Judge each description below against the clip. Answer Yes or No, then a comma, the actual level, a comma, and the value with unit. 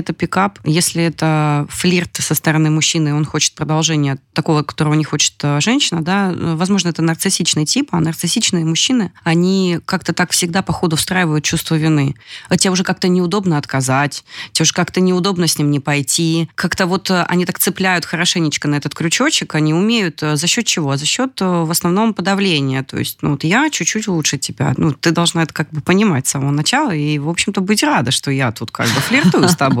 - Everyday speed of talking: No, fast, 195 wpm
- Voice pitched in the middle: Yes, medium, 165 Hz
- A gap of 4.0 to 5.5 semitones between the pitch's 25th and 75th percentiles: No, average, 3.4 semitones